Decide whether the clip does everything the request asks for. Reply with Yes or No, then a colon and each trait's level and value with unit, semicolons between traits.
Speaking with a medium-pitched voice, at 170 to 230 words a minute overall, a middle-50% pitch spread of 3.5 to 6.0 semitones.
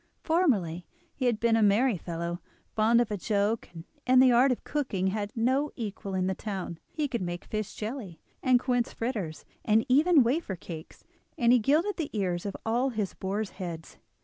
No: high, 220 Hz; average, 190 wpm; average, 5.1 semitones